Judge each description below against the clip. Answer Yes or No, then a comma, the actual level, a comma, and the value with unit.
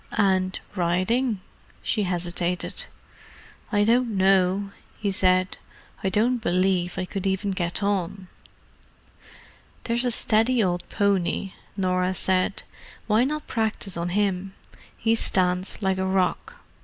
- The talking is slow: Yes, slow, 120 wpm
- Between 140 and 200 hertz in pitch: Yes, high, 190 Hz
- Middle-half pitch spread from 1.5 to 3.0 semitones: Yes, narrow, 2.4 semitones